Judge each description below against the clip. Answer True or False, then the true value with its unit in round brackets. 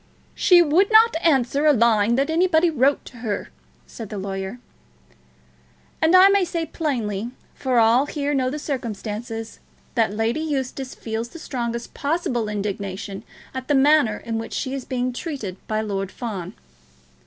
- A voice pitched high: True (245 Hz)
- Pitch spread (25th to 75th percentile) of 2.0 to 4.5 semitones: False (5.3 semitones)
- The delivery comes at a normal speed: True (155 wpm)